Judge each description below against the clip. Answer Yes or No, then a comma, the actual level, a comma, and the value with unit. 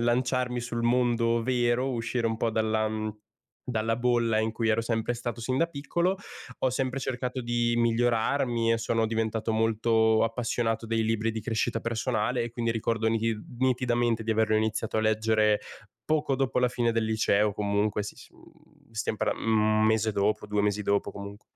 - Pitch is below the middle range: Yes, low, 115 Hz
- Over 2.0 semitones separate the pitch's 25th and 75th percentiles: No, narrow, 1.7 semitones